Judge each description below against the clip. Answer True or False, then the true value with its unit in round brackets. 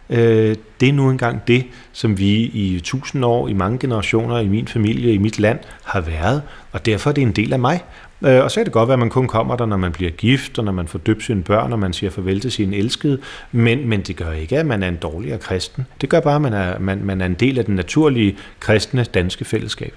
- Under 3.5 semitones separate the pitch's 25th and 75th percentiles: False (4.3 semitones)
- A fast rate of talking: True (260 wpm)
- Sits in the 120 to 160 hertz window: False (110 Hz)